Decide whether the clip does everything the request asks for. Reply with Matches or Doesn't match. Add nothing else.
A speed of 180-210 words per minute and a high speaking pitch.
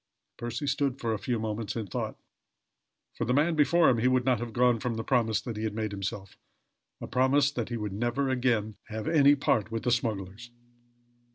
Doesn't match